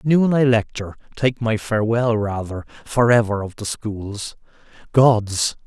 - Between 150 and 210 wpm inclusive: No, average, 140 wpm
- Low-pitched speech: Yes, low, 110 Hz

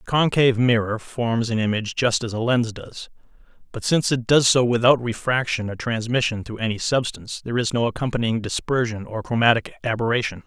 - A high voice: No, low, 115 Hz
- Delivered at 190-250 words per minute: No, average, 180 wpm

